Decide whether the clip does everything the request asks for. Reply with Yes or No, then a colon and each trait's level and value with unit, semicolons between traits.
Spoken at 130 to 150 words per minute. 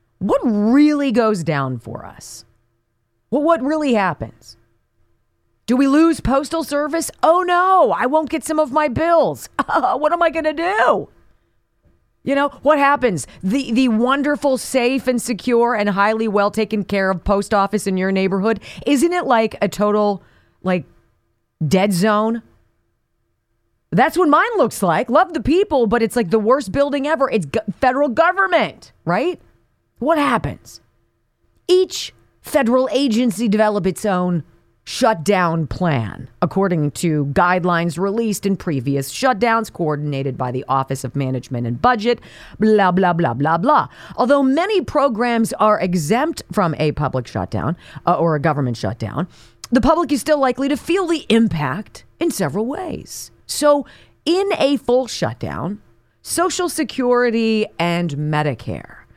Yes: average, 145 wpm